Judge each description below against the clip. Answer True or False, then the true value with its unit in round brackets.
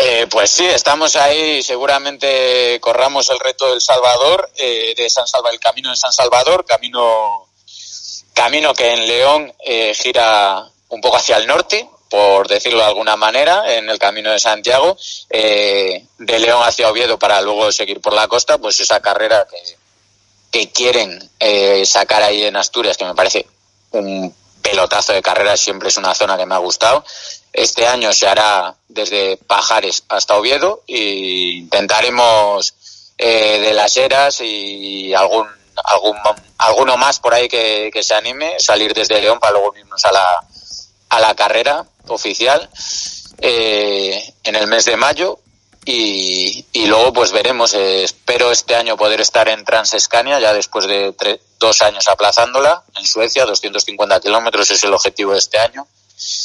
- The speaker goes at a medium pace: True (160 wpm)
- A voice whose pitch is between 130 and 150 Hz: False (110 Hz)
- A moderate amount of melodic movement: False (5.9 semitones)